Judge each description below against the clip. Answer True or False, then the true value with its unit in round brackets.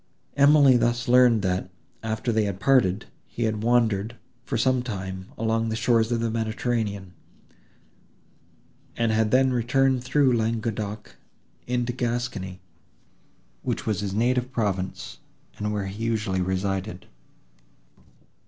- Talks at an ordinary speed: False (125 wpm)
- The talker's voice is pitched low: True (115 Hz)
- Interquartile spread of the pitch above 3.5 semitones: False (3.2 semitones)